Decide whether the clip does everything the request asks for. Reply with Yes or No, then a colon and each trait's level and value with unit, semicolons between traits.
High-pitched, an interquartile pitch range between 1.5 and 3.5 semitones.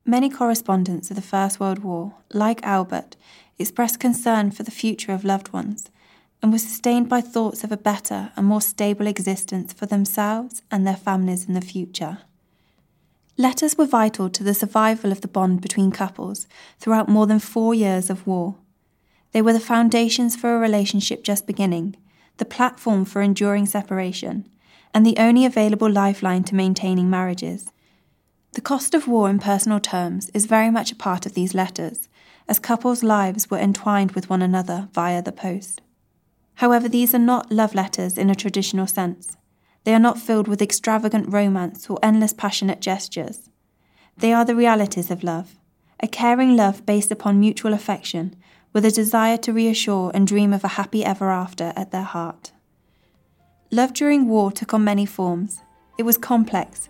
Yes: high, 205 Hz; average, 2.8 semitones